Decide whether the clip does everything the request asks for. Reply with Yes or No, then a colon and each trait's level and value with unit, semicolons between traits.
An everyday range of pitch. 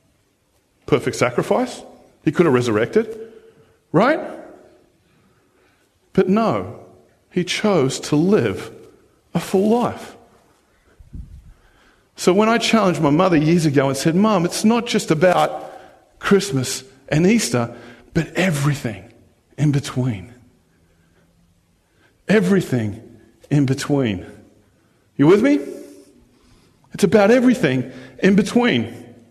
No: wide, 9.0 semitones